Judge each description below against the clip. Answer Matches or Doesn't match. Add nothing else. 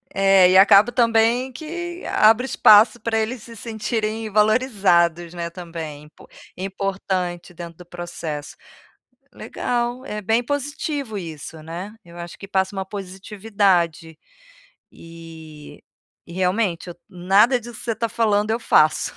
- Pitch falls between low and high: Doesn't match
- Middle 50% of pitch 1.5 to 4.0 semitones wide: Doesn't match